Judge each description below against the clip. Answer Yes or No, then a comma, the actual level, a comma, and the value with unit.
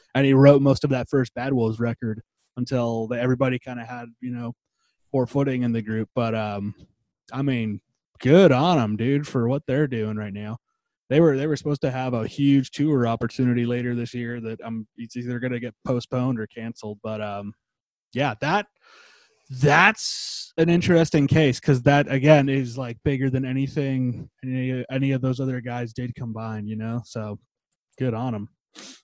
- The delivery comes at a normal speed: Yes, average, 190 wpm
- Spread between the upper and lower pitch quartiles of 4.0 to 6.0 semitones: No, average, 2.9 semitones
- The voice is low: Yes, low, 125 Hz